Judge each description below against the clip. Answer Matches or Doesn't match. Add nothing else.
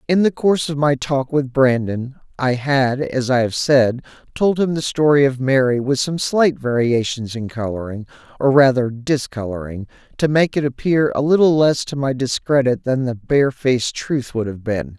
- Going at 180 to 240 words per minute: Matches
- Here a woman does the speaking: Doesn't match